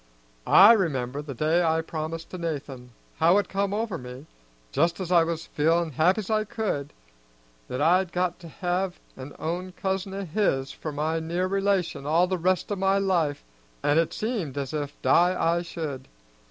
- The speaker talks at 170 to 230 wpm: Yes, average, 175 wpm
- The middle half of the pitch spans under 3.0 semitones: No, average, 3.8 semitones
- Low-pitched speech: No, medium, 170 Hz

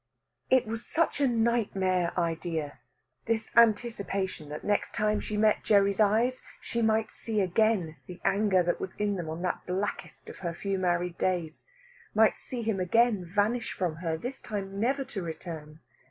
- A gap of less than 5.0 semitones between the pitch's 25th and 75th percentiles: Yes, average, 4.1 semitones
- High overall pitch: Yes, high, 200 Hz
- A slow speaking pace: No, average, 170 wpm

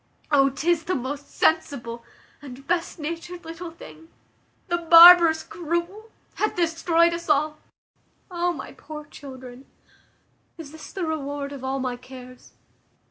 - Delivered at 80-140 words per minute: Yes, slow, 135 wpm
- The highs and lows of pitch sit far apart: No, average, 3.7 semitones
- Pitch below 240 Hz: No, very high, 315 Hz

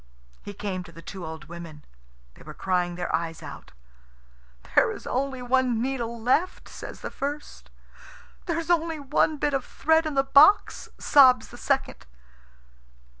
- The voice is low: No, very high, 255 Hz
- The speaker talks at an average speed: Yes, average, 160 wpm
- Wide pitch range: Yes, wide, 8.1 semitones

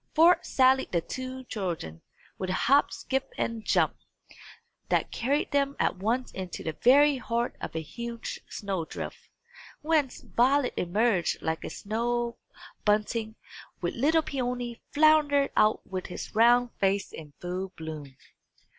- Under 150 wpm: Yes, average, 140 wpm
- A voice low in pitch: No, high, 235 Hz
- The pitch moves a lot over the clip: Yes, wide, 5.9 semitones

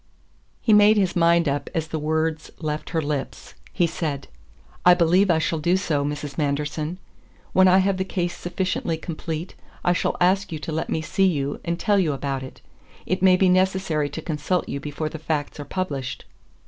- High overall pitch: No, medium, 165 Hz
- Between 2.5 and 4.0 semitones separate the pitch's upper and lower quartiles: Yes, average, 3.6 semitones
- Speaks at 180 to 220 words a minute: Yes, average, 195 wpm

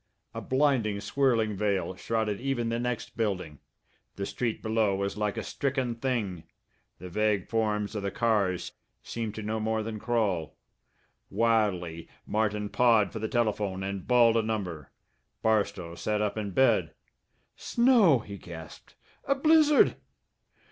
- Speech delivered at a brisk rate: No, average, 140 wpm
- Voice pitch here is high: No, low, 110 Hz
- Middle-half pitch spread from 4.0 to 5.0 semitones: No, average, 2.9 semitones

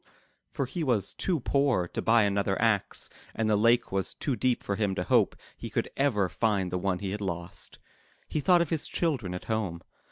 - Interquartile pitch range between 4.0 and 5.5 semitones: Yes, average, 5.0 semitones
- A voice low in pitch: Yes, low, 105 Hz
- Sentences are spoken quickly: Yes, fast, 215 wpm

